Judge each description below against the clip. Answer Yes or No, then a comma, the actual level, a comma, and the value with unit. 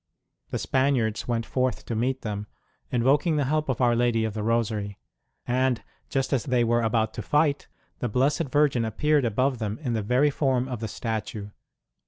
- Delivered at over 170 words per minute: Yes, average, 185 wpm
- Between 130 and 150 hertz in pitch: No, low, 120 Hz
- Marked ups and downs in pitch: No, average, 3.3 semitones